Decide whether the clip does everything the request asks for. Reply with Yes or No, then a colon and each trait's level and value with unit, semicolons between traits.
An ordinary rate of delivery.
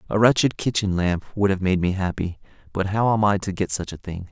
No: fast, 250 wpm